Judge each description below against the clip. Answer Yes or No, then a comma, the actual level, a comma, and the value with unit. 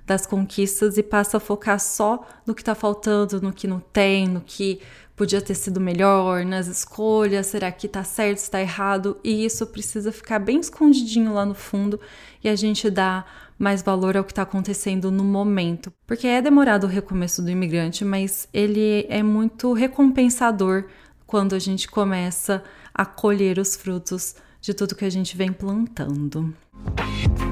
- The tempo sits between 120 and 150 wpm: No, average, 170 wpm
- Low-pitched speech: No, high, 200 Hz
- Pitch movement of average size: No, narrow, 2.0 semitones